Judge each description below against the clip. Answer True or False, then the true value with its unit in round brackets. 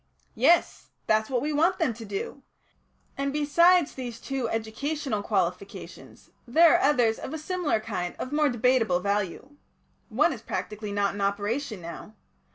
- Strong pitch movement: True (6.1 semitones)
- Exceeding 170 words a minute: False (160 wpm)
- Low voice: False (235 Hz)